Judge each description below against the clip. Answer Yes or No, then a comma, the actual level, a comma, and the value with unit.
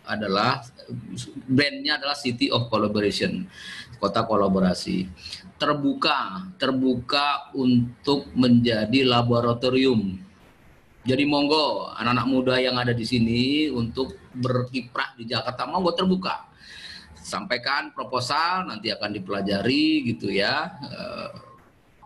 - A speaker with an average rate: Yes, average, 95 wpm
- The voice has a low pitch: Yes, low, 125 Hz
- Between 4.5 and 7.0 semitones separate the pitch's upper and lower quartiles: No, average, 3.4 semitones